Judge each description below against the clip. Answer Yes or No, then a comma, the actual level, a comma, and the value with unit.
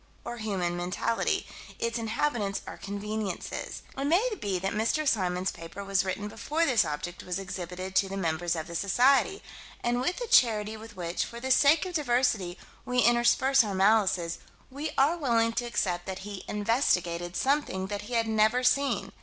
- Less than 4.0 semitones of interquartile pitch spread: No, average, 4.9 semitones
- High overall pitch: Yes, high, 215 Hz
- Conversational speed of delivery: Yes, average, 175 wpm